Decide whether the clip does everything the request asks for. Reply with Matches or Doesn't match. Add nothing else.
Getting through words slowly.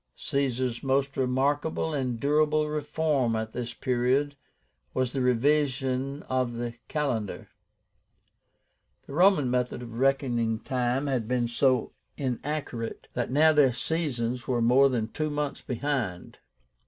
Matches